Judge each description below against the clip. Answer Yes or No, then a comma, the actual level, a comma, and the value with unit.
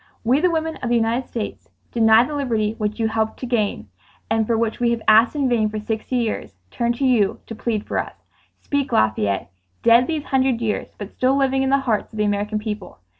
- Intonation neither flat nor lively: Yes, average, 3.2 semitones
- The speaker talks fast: Yes, fast, 225 wpm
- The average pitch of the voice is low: No, high, 230 Hz